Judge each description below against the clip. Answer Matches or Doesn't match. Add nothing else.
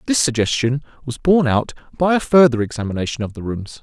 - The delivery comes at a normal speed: Matches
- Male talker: Matches